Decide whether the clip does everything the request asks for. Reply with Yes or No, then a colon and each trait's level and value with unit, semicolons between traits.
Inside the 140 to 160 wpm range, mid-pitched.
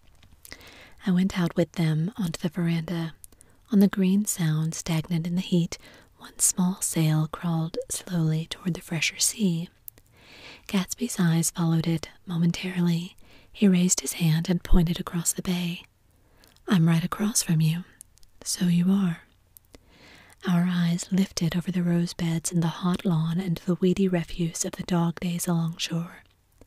Yes: average, 155 wpm; medium, 175 Hz